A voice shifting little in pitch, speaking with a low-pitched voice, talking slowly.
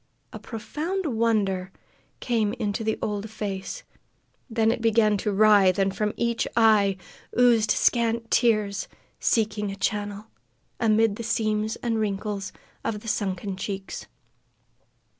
No: narrow, 2.1 semitones; high, 215 Hz; slow, 125 wpm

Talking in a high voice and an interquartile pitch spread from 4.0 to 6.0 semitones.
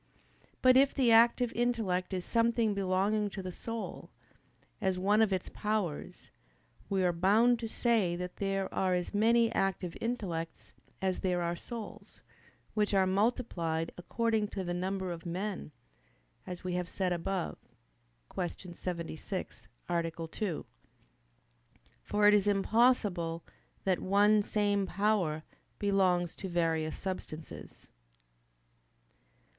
No: high, 195 Hz; average, 3.3 semitones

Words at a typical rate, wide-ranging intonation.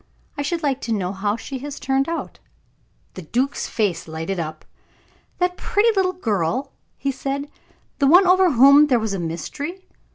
Yes: average, 170 wpm; wide, 7.3 semitones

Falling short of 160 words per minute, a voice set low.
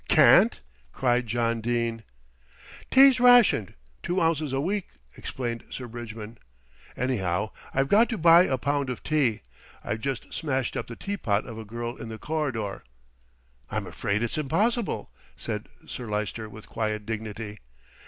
Yes: average, 145 wpm; low, 120 Hz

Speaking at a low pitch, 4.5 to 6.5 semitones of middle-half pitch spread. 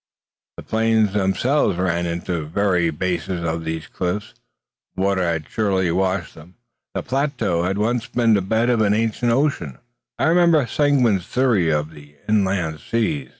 Yes: very low, 95 Hz; average, 5.1 semitones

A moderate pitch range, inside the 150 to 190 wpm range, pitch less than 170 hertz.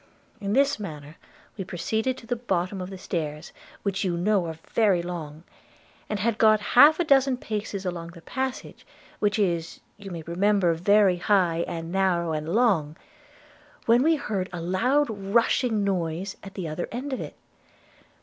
No: average, 4.5 semitones; average, 170 wpm; high, 195 Hz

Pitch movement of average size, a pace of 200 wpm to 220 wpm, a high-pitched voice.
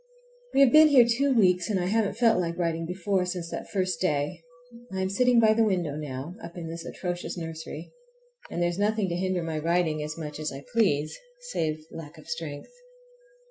No: average, 4.0 semitones; fast, 205 wpm; medium, 175 Hz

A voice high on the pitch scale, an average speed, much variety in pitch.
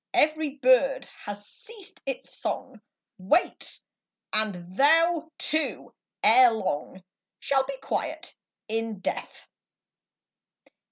No: very high, 260 Hz; slow, 95 wpm; wide, 6.4 semitones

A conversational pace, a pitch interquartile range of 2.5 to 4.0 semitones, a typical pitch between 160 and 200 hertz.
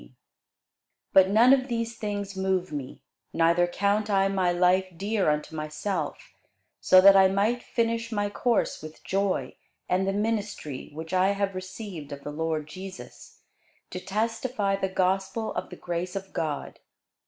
Yes: average, 165 wpm; average, 2.8 semitones; high, 190 Hz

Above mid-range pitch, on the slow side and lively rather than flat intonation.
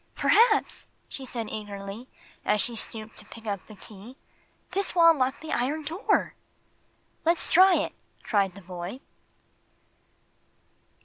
Yes: high, 235 Hz; slow, 130 wpm; wide, 7.6 semitones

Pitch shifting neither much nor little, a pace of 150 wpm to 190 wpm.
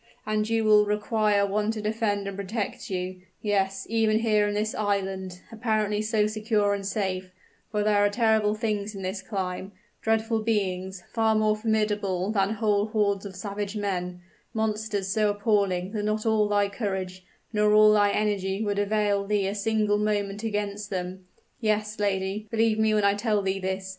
No: narrow, 1.5 semitones; average, 175 wpm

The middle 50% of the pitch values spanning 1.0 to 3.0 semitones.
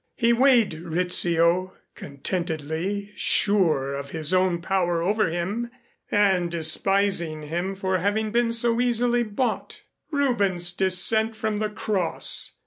No: average, 4.2 semitones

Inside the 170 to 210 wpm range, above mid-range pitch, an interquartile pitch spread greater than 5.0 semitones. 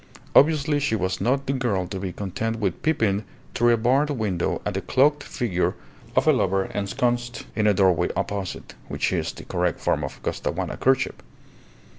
No: average, 175 wpm; low, 110 Hz; wide, 5.4 semitones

